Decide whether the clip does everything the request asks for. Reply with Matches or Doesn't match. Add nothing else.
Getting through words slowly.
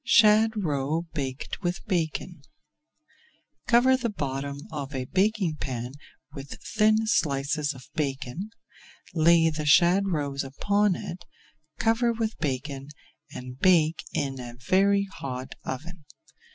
Matches